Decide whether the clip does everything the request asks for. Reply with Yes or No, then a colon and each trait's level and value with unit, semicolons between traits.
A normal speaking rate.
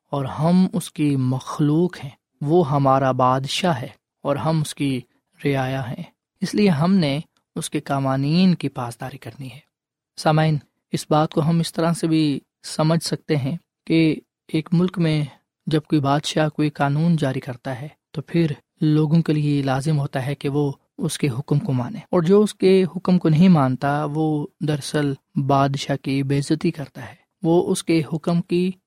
Yes: average, 180 wpm